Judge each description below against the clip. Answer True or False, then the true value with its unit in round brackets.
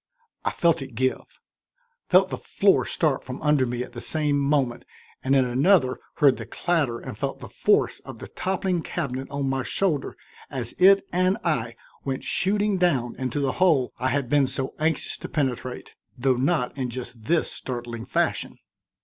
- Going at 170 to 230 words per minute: True (175 wpm)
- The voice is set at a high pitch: False (135 Hz)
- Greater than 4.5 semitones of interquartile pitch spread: True (4.9 semitones)